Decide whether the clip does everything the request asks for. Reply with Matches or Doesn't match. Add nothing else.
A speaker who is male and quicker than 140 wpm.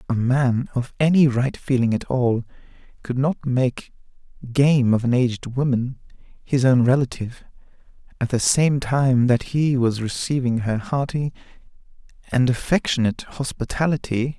Doesn't match